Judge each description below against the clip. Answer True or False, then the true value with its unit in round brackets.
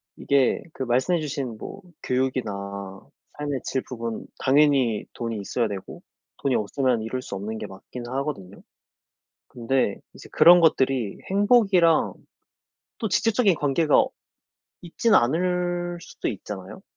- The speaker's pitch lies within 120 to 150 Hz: True (135 Hz)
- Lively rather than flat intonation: True (6.8 semitones)